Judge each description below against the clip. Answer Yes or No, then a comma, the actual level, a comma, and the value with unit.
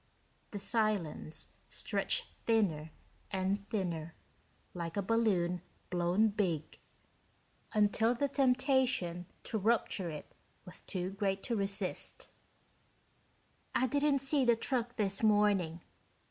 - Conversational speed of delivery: No, slow, 105 wpm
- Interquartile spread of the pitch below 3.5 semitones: No, average, 4.4 semitones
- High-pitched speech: Yes, high, 205 Hz